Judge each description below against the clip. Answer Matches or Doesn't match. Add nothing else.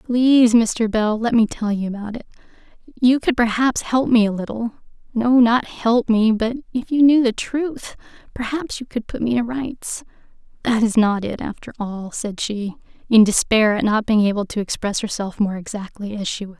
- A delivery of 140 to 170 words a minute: Doesn't match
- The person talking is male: Doesn't match